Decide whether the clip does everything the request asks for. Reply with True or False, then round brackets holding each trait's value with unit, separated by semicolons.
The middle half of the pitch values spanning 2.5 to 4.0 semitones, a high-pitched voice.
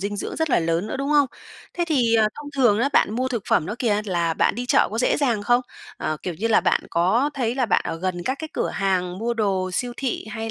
False (5.3 semitones; 225 Hz)